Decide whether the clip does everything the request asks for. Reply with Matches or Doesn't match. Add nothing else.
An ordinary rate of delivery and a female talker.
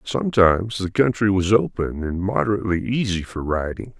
Doesn't match